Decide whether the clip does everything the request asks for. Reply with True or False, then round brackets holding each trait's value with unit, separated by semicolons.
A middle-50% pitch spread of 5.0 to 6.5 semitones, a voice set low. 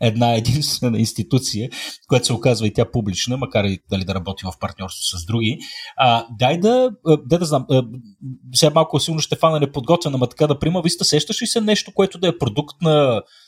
True (5.5 semitones; 130 Hz)